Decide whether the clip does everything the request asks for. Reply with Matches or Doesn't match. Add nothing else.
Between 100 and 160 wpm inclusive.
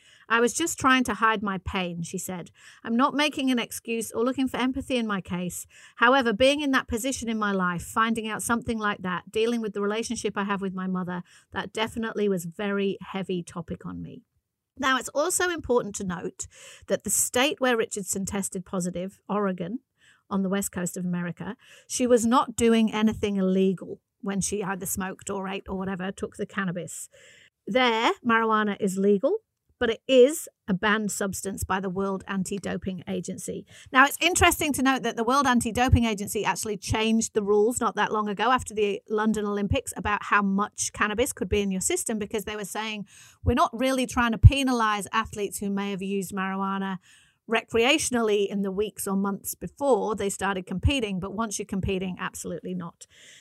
Doesn't match